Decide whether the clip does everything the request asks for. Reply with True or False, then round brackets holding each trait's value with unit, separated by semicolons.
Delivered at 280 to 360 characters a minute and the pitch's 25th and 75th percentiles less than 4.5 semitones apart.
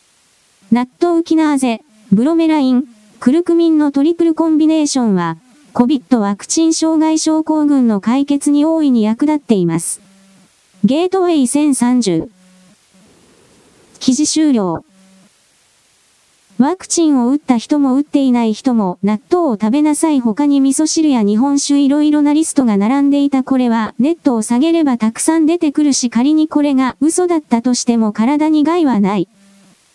False (315 characters per minute; 5.6 semitones)